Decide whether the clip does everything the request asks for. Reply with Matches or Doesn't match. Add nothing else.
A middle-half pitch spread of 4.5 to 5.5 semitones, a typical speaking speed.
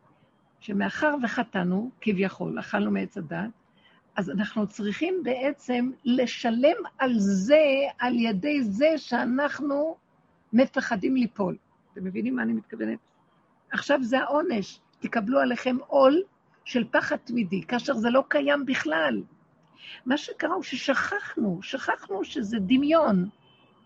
Matches